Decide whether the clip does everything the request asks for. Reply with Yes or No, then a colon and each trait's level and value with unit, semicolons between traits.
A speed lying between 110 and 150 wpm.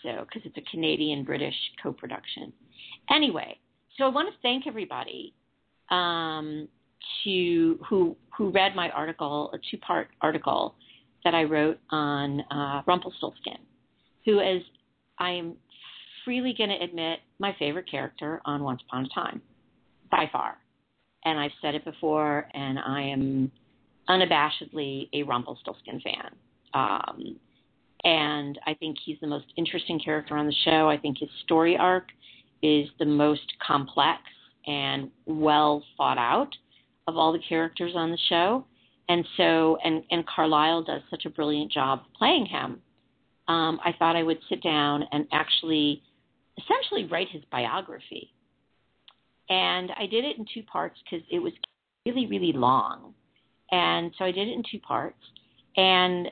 Yes: average, 145 wpm